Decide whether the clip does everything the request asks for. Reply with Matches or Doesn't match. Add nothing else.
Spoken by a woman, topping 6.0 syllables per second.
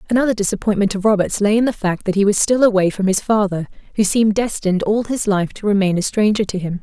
Matches